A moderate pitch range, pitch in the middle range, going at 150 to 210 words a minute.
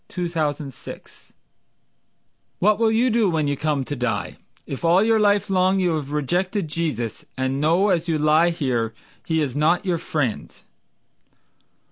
Yes: average, 4.5 semitones; medium, 160 Hz; average, 160 wpm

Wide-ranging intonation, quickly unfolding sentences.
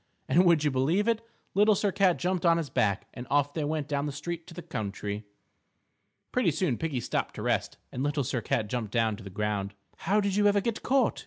Yes: wide, 7.4 semitones; fast, 230 wpm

